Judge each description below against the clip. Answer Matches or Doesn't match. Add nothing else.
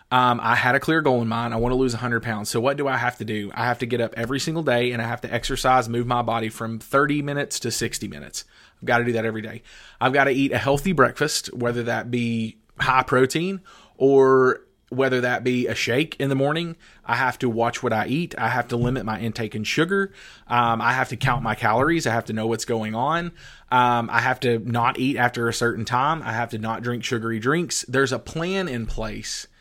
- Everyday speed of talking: Doesn't match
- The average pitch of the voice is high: Doesn't match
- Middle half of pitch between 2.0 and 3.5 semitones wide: Matches